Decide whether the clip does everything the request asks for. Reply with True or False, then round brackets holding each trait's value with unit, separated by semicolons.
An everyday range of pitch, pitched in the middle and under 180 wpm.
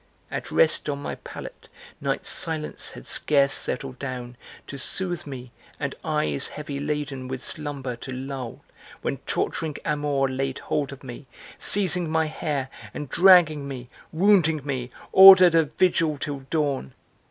True (3.1 semitones; 145 Hz; 145 wpm)